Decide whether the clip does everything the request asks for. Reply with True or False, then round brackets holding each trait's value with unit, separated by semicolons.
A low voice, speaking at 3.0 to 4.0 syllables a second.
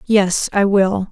False (195 Hz; 3.2 syllables/s)